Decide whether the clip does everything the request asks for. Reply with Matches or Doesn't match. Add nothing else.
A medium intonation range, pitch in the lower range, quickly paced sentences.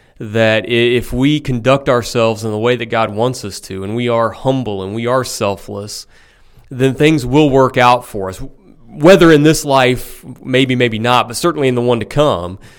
Doesn't match